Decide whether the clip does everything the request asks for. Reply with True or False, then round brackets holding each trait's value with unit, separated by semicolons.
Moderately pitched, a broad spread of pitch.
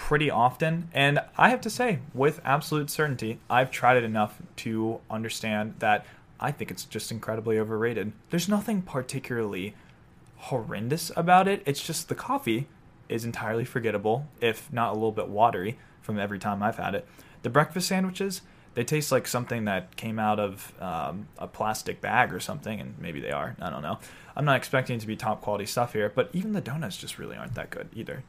False (125 Hz; 5.7 semitones)